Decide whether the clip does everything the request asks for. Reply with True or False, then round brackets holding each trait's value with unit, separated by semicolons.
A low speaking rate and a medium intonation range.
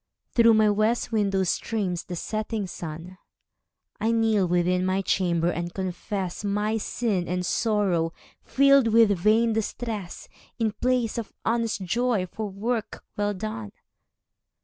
True (130 wpm; 3.7 semitones)